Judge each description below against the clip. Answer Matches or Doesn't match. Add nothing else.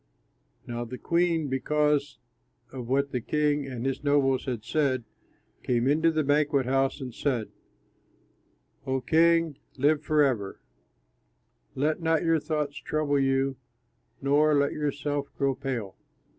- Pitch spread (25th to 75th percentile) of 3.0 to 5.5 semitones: Doesn't match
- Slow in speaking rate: Matches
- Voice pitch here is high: Doesn't match